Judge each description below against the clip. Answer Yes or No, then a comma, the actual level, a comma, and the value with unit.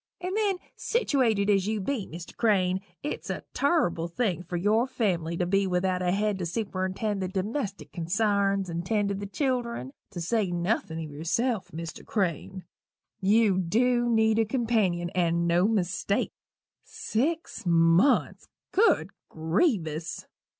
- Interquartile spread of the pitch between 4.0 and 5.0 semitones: Yes, average, 4.5 semitones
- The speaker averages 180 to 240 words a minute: No, average, 145 wpm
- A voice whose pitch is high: Yes, high, 195 Hz